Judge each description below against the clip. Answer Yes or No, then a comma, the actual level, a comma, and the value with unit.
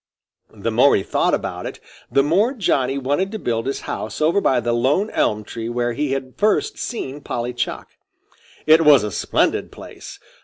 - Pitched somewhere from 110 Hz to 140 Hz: Yes, low, 135 Hz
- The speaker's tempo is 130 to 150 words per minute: No, average, 185 wpm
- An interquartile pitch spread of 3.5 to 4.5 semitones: No, average, 5.1 semitones